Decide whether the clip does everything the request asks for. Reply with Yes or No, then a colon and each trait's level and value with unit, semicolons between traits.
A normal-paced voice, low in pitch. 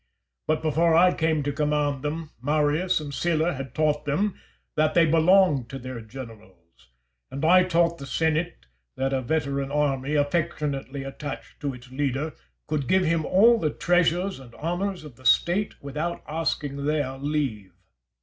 No: average, 160 wpm; medium, 150 Hz